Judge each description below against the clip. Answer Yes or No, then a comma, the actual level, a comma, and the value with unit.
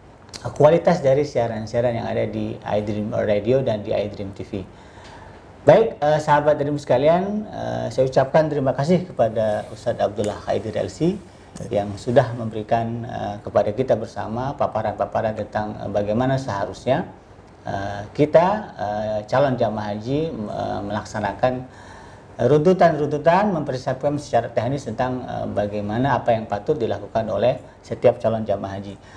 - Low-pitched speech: Yes, low, 115 Hz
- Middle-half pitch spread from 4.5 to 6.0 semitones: Yes, average, 4.8 semitones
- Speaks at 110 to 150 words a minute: Yes, average, 130 wpm